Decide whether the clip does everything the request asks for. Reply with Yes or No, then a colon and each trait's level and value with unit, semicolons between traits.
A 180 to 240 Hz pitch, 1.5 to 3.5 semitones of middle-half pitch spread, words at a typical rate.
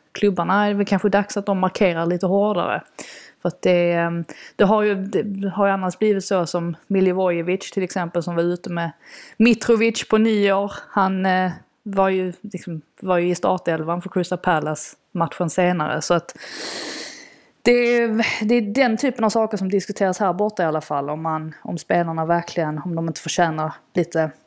Yes: medium, 185 Hz; average, 3.2 semitones; average, 185 wpm